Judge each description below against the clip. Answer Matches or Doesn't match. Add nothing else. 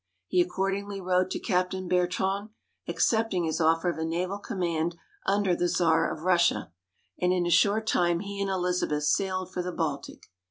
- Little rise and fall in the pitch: Matches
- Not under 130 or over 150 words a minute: Doesn't match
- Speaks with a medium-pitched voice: Matches